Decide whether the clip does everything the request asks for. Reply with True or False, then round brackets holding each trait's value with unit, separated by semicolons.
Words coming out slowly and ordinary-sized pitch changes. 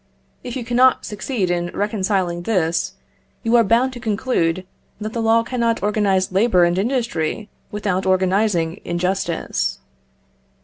True (130 wpm; 4.2 semitones)